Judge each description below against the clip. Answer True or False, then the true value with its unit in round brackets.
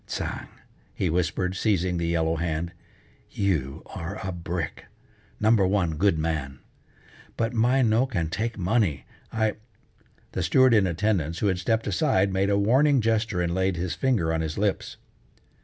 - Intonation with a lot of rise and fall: False (4.7 semitones)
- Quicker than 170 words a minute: False (160 wpm)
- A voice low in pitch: True (95 Hz)